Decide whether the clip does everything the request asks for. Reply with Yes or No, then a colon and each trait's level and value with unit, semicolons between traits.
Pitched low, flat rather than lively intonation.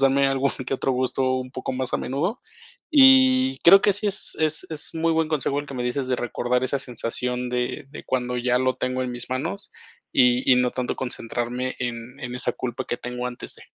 Yes: low, 130 Hz; narrow, 2.2 semitones